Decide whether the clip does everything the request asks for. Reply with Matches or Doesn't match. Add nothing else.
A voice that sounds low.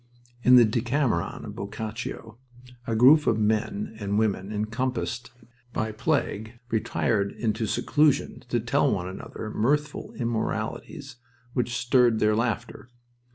Matches